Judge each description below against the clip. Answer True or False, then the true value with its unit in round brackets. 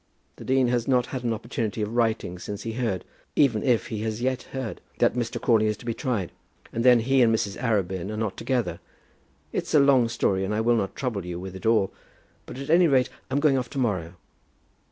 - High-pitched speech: False (115 Hz)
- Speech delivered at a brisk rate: True (225 wpm)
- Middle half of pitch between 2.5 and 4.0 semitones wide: True (3.4 semitones)